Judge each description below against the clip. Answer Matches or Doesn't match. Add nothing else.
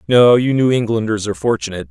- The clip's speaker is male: Matches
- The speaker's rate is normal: Matches